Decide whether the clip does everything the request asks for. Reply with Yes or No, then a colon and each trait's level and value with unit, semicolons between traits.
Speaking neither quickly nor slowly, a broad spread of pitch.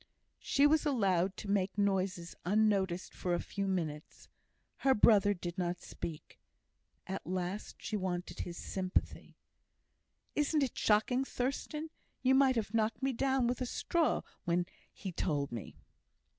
Yes: average, 145 wpm; wide, 6.0 semitones